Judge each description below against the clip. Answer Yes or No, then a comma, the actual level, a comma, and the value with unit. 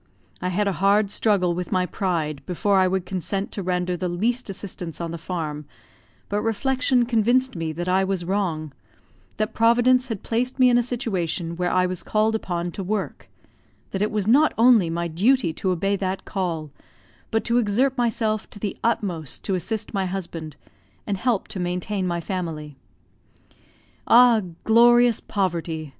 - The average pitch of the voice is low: No, high, 195 Hz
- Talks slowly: No, average, 170 wpm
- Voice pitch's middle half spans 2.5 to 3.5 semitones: No, average, 4.3 semitones